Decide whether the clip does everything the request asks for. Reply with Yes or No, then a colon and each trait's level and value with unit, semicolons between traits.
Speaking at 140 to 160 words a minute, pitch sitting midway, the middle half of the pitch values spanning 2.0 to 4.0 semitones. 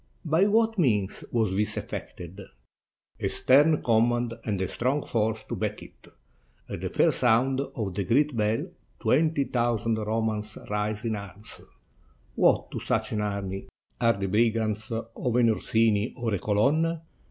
No: average, 155 wpm; low, 115 Hz; average, 3.4 semitones